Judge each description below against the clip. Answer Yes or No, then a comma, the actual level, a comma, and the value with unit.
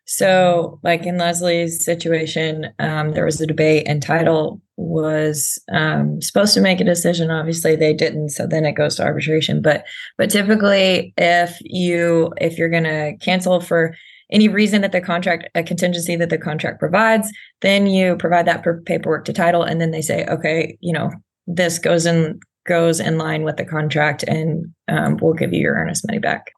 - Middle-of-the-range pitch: Yes, medium, 170 Hz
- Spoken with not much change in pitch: Yes, narrow, 2.0 semitones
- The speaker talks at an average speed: Yes, average, 185 wpm